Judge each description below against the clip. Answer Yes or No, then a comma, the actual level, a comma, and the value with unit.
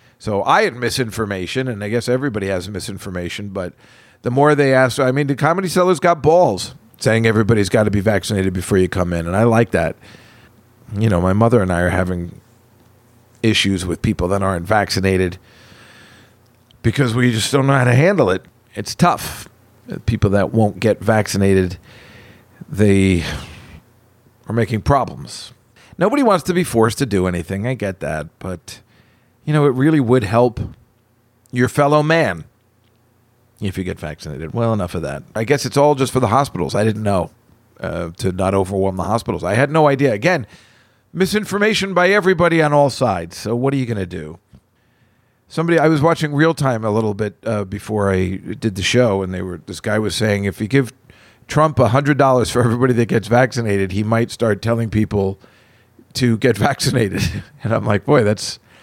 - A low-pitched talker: Yes, low, 115 Hz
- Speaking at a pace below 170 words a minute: No, average, 185 wpm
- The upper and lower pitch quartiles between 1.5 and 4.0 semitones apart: No, average, 4.4 semitones